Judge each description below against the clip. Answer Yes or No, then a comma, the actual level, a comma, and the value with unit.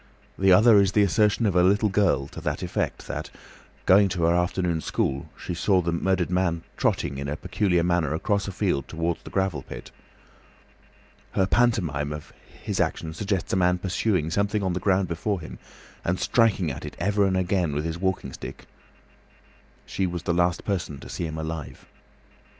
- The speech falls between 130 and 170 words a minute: No, average, 185 wpm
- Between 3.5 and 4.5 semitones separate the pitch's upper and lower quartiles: No, average, 3.0 semitones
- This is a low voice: Yes, very low, 90 Hz